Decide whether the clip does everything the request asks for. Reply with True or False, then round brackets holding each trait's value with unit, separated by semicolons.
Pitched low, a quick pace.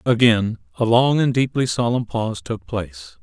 False (110 Hz; 165 wpm)